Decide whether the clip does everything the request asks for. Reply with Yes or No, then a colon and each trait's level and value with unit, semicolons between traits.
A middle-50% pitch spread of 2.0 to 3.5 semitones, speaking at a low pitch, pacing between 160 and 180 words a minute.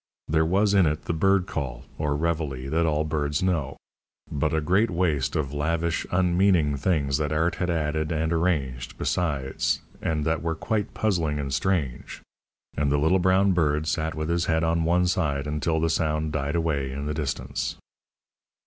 Yes: average, 2.7 semitones; very low, 80 Hz; average, 175 wpm